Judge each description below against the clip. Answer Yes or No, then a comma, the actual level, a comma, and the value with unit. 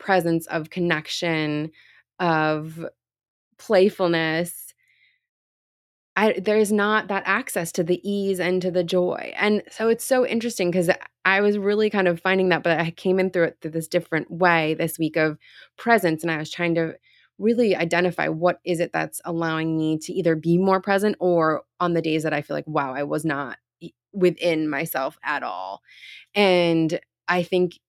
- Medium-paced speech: Yes, average, 175 wpm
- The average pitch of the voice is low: No, medium, 175 Hz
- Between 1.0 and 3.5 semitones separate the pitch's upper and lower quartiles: Yes, average, 2.9 semitones